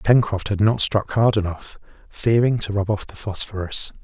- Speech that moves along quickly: No, average, 180 wpm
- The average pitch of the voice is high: No, low, 105 Hz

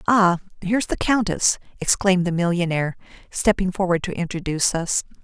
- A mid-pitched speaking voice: Yes, medium, 180 Hz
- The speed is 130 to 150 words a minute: Yes, slow, 135 wpm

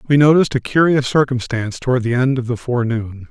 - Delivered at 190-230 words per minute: Yes, average, 200 wpm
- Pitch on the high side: No, low, 125 Hz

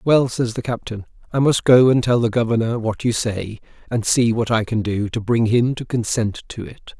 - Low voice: Yes, low, 115 Hz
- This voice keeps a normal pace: No, fast, 230 wpm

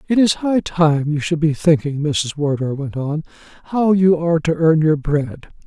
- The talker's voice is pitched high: No, medium, 160 Hz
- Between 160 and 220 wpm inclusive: Yes, average, 200 wpm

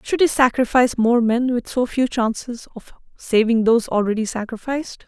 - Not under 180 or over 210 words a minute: No, average, 165 wpm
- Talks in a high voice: Yes, high, 235 Hz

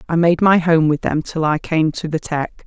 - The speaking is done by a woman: Yes, female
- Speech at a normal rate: No, fast, 270 wpm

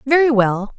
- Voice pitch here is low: No, very high, 250 Hz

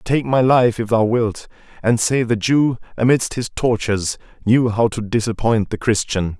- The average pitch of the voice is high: No, low, 115 Hz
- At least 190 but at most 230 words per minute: No, average, 180 wpm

